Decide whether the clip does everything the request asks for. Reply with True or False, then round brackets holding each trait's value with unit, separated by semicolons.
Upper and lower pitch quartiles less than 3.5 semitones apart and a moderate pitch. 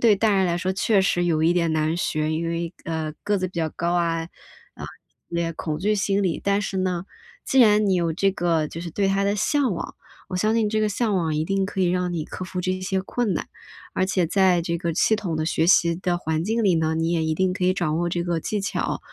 True (2.9 semitones; 180 Hz)